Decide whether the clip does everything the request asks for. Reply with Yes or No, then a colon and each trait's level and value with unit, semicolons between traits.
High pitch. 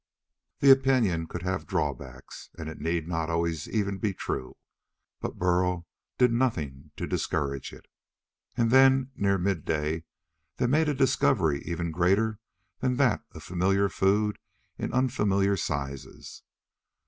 No: very low, 95 Hz